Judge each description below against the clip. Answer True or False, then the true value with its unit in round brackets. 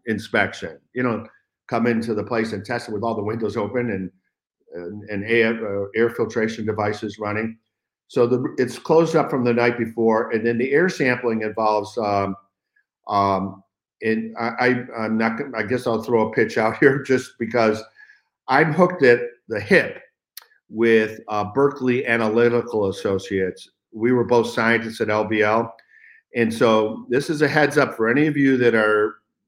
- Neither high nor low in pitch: False (115 Hz)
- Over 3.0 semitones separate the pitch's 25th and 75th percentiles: False (2.5 semitones)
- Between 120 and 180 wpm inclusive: True (175 wpm)